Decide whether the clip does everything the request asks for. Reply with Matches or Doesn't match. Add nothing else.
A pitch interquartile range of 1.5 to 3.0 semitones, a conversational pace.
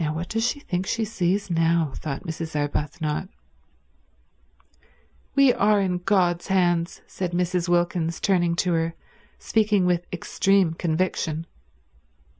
Doesn't match